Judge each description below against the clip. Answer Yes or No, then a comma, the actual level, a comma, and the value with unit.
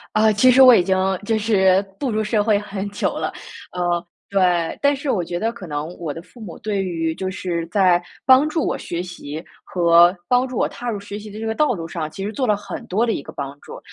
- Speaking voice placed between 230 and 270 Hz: No, high, 200 Hz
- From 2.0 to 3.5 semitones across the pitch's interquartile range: No, average, 4.2 semitones